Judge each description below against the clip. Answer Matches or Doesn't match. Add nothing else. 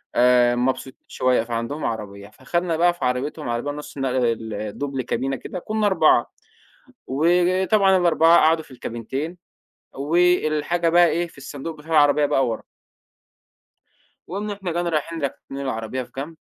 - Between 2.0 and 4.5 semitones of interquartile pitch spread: Doesn't match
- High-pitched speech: Doesn't match